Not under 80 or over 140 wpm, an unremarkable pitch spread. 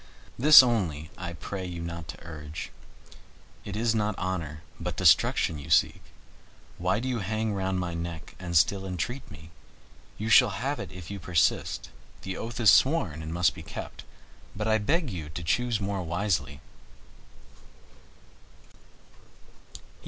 No: average, 150 wpm; average, 4.7 semitones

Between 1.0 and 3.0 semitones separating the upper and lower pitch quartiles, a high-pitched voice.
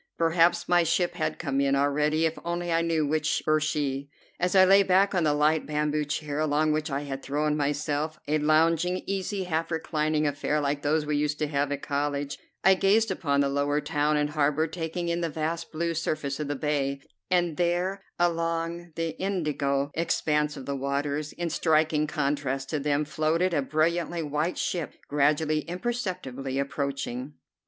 No: narrow, 2.6 semitones; medium, 155 Hz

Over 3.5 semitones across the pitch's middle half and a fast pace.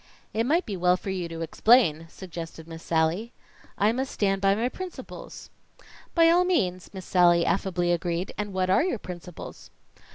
No: average, 4.6 semitones; average, 170 wpm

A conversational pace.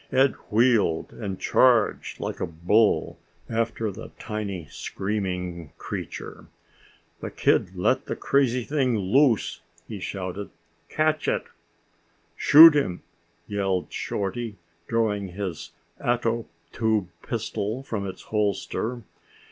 No: slow, 110 wpm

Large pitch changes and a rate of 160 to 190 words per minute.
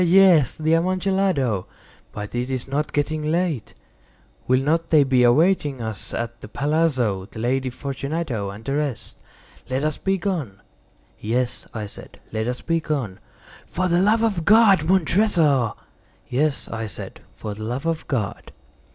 Yes: wide, 5.8 semitones; average, 170 wpm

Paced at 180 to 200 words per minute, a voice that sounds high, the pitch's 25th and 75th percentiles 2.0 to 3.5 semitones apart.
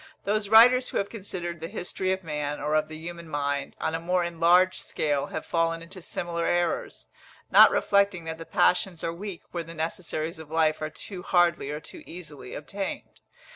No: average, 190 wpm; medium, 170 Hz; average, 2.8 semitones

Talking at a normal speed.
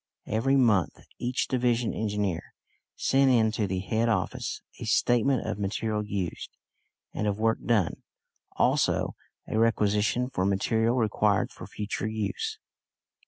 No: slow, 130 wpm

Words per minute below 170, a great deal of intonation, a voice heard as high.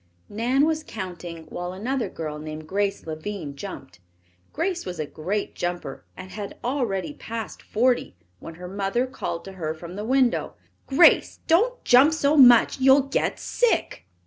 Yes: average, 155 wpm; wide, 7.6 semitones; high, 205 Hz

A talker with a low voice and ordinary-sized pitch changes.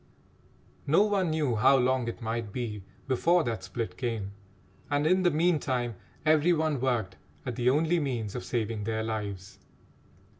No: low, 125 Hz; wide, 5.7 semitones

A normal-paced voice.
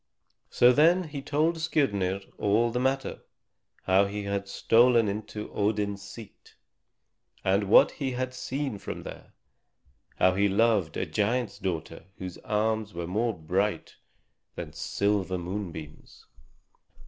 No: slow, 125 wpm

